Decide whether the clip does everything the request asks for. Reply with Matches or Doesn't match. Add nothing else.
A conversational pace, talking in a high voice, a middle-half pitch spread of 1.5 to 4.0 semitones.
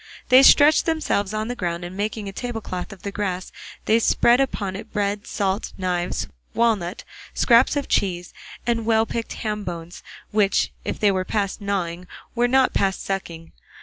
Matches